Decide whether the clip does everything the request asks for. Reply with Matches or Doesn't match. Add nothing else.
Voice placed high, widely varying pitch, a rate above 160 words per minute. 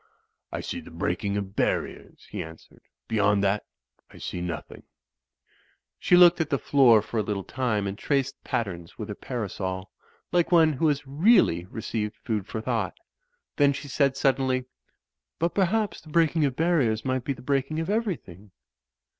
Doesn't match